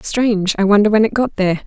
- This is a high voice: Yes, high, 210 Hz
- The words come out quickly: Yes, fast, 215 wpm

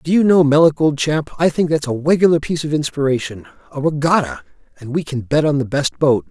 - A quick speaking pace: Yes, fast, 230 wpm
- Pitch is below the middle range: No, medium, 145 Hz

